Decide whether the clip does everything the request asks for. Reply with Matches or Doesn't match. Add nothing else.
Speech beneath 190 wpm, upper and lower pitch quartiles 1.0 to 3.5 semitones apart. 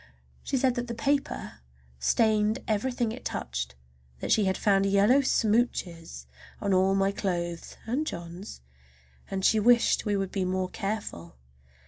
Doesn't match